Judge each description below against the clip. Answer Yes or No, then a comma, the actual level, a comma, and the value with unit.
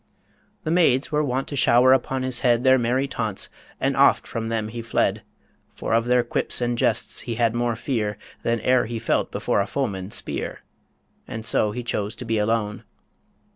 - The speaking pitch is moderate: No, low, 120 Hz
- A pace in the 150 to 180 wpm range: No, average, 190 wpm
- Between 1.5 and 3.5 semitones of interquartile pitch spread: Yes, narrow, 2.4 semitones